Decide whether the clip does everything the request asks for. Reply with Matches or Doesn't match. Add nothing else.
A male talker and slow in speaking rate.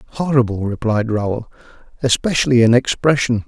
Matches